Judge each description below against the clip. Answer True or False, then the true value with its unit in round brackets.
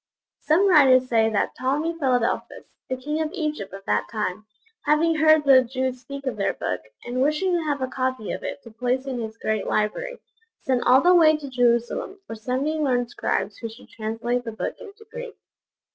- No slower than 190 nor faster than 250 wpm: True (195 wpm)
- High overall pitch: True (260 Hz)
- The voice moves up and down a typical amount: True (4.6 semitones)